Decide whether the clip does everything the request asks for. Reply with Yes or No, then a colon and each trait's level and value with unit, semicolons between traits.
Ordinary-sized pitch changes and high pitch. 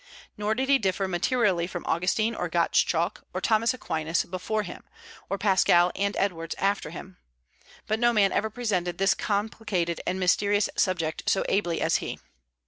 Yes: average, 3.5 semitones; high, 195 Hz